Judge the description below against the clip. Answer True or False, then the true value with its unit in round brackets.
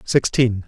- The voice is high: False (120 Hz)